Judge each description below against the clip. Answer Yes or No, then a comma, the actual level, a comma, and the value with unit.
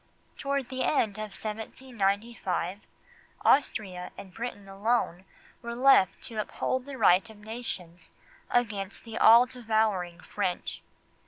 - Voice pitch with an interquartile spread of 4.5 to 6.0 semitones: No, average, 3.8 semitones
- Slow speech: Yes, slow, 115 wpm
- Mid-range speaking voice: No, high, 220 Hz